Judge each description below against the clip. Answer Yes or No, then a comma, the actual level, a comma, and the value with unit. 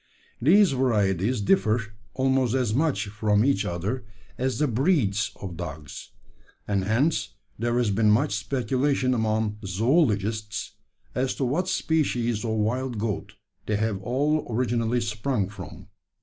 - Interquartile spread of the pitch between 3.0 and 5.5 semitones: Yes, average, 4.1 semitones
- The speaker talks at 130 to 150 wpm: Yes, slow, 135 wpm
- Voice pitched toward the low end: Yes, low, 115 Hz